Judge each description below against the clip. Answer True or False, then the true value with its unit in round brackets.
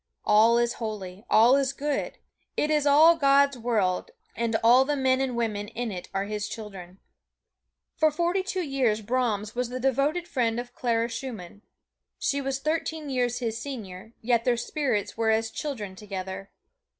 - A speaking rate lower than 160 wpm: False (165 wpm)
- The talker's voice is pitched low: False (240 Hz)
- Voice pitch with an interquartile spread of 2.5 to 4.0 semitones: False (4.4 semitones)